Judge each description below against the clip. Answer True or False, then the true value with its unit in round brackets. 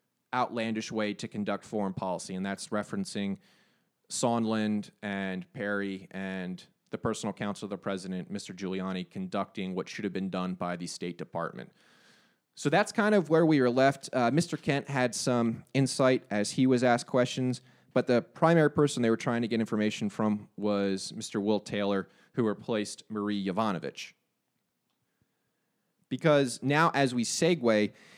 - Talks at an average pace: True (160 wpm)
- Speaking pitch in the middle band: False (110 Hz)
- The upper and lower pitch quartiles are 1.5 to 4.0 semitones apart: False (4.6 semitones)